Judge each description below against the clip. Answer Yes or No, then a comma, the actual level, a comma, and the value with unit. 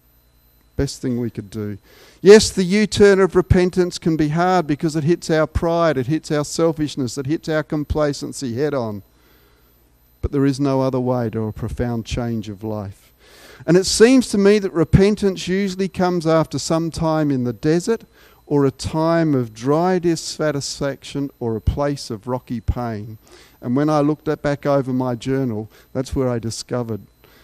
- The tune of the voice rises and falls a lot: Yes, wide, 5.8 semitones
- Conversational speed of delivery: Yes, average, 175 wpm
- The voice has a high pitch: No, medium, 140 Hz